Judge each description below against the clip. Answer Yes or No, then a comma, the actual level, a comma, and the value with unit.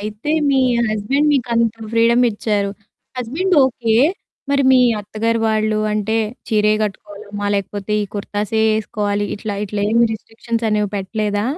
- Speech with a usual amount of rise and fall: No, narrow, 2.0 semitones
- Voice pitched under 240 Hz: Yes, high, 215 Hz